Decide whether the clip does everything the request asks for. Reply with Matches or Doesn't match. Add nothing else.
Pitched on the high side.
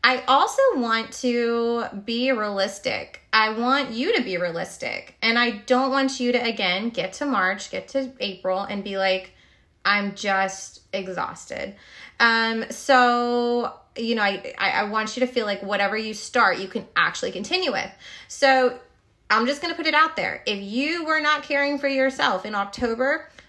Matches